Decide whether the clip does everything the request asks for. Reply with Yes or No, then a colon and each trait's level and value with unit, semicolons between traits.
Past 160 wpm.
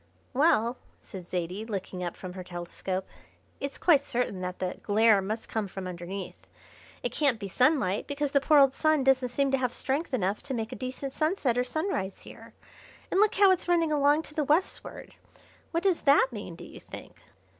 Yes: average, 195 wpm